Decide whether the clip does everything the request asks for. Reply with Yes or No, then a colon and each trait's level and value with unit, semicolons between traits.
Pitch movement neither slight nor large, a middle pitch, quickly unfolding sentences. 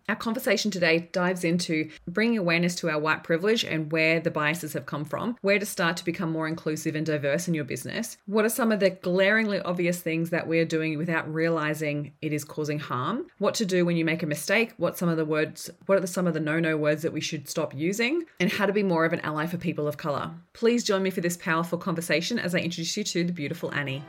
Yes: average, 3.5 semitones; medium, 170 Hz; fast, 250 wpm